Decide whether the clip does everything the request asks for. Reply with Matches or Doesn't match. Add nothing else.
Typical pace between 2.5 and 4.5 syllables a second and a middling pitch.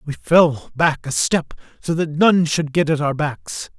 Matches